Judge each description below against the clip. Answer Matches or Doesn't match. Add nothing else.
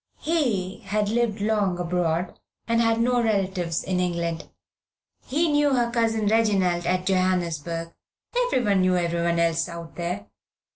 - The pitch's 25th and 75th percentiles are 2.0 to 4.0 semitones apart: Doesn't match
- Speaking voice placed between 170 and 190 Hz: Matches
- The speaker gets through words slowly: Matches